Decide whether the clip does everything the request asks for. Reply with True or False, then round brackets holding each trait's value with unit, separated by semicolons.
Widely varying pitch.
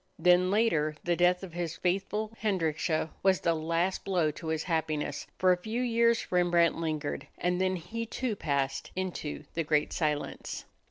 False (3.0 semitones)